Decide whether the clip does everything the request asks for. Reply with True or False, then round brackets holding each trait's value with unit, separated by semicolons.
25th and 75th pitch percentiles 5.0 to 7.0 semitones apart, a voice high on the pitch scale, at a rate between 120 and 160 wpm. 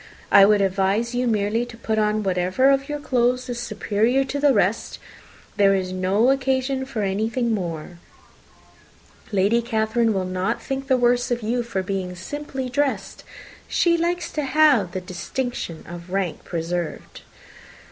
True (5.3 semitones; 225 Hz; 155 wpm)